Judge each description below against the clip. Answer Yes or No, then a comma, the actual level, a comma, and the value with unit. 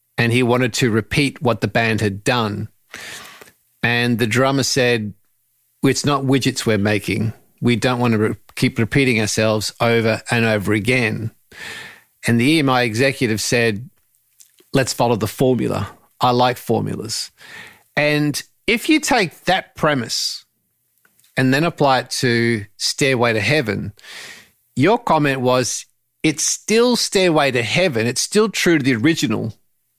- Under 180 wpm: Yes, average, 140 wpm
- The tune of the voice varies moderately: Yes, average, 3.5 semitones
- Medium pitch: No, low, 125 Hz